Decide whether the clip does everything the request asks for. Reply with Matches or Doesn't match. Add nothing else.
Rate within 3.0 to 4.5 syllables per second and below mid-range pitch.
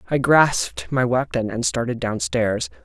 Matches